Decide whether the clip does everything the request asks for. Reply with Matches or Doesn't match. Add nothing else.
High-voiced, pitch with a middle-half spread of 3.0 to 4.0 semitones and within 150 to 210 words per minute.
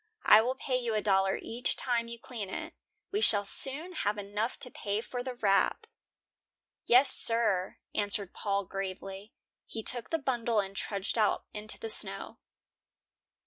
Matches